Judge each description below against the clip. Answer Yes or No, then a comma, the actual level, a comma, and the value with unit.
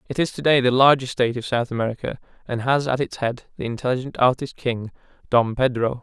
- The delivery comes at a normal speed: No, fast, 210 wpm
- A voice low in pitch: Yes, low, 125 Hz